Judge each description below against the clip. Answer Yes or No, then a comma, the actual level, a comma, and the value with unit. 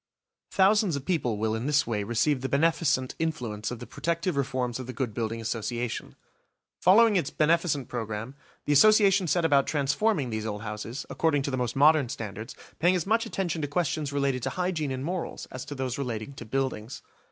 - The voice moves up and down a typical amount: No, wide, 5.7 semitones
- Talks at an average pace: Yes, average, 190 wpm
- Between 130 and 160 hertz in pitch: Yes, medium, 140 Hz